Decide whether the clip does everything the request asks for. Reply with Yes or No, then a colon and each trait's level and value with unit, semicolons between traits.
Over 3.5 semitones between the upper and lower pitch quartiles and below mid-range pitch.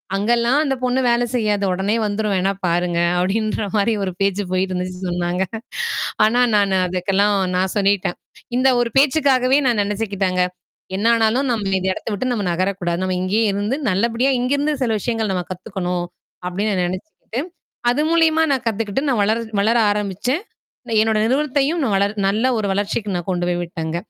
No: average, 4.4 semitones; high, 205 Hz